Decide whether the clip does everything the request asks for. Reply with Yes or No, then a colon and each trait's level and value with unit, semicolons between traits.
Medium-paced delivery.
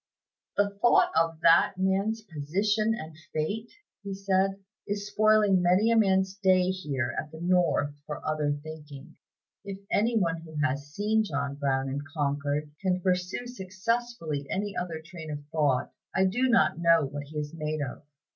Yes: average, 165 wpm